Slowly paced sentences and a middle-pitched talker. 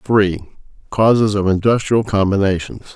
No: slow, 100 wpm; low, 100 Hz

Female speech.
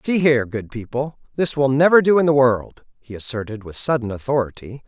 No: male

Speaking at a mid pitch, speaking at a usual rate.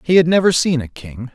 No: medium, 145 Hz; fast, 270 wpm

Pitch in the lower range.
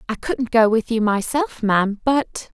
No: high, 230 Hz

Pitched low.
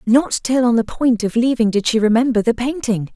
No: high, 235 Hz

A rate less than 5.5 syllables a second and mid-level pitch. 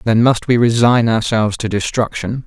No: 5.1 syllables/s; low, 115 Hz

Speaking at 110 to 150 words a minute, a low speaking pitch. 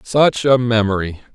Yes: slow, 135 wpm; low, 115 Hz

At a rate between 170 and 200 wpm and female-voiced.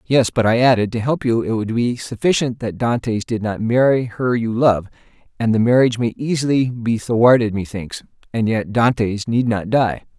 No: average, 195 wpm; male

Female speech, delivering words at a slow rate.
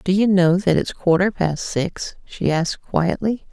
No: female; average, 190 wpm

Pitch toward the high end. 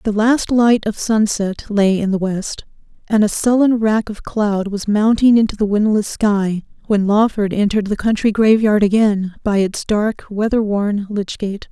Yes: high, 210 Hz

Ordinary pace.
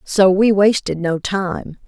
Yes: average, 160 wpm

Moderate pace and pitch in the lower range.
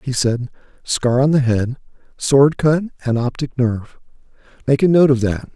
Yes: average, 160 wpm; low, 130 Hz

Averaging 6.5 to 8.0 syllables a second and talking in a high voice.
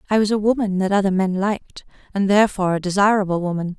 Yes: 6.9 syllables/s; high, 195 Hz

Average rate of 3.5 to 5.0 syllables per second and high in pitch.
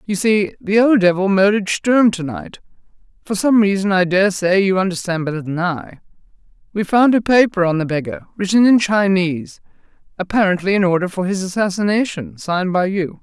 No: 5.5 syllables/s; high, 195 Hz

